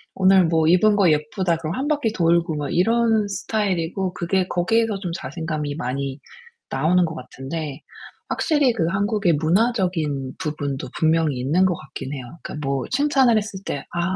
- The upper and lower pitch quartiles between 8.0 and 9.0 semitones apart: No, average, 5.1 semitones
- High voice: No, medium, 175 Hz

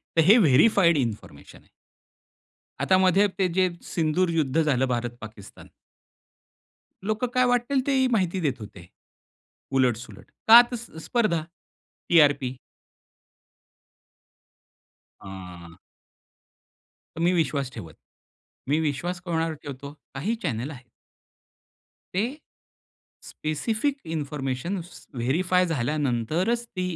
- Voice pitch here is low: No, medium, 155 Hz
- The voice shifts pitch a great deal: Yes, wide, 6.5 semitones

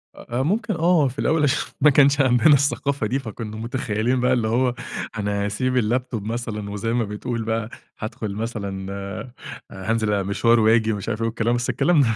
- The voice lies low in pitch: Yes, low, 115 Hz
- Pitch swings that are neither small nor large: Yes, average, 3.4 semitones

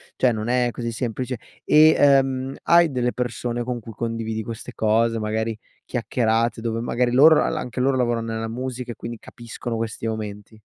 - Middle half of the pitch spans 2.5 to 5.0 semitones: No, narrow, 2.0 semitones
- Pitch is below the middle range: Yes, low, 120 Hz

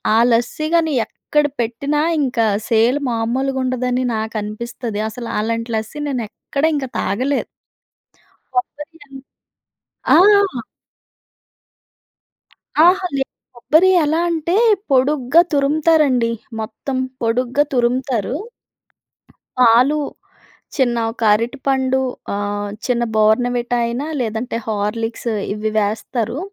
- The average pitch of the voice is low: No, high, 245 Hz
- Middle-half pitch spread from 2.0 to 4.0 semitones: Yes, average, 3.6 semitones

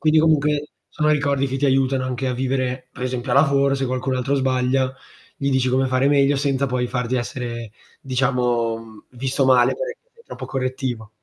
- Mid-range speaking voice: No, low, 130 Hz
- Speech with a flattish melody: Yes, narrow, 1.7 semitones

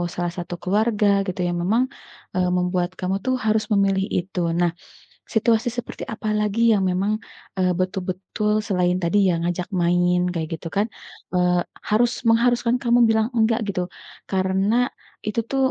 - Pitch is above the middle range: Yes, high, 195 Hz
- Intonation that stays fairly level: No, average, 3.5 semitones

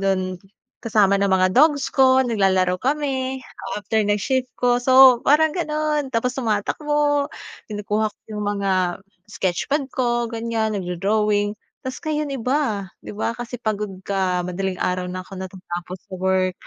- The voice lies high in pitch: Yes, high, 215 Hz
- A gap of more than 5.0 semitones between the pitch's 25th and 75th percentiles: Yes, wide, 5.5 semitones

